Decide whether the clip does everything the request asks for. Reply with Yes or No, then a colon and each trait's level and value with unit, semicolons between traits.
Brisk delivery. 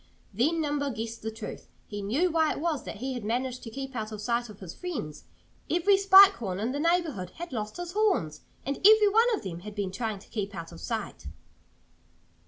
Yes: fast, 215 wpm